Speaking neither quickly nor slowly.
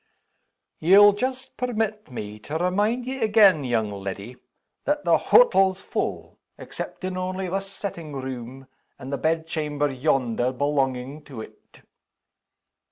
No: slow, 120 wpm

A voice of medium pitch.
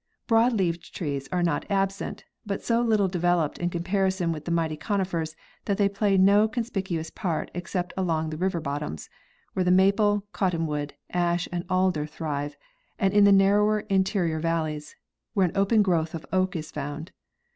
Yes: medium, 180 Hz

